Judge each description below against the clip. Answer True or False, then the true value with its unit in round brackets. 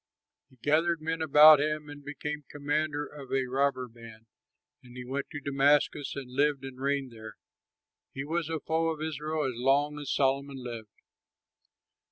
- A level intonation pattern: True (2.3 semitones)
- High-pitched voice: False (145 Hz)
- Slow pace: False (165 wpm)